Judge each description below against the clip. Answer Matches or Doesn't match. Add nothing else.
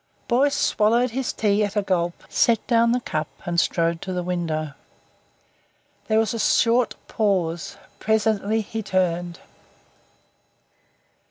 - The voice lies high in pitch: Matches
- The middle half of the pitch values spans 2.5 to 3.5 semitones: Doesn't match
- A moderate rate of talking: Doesn't match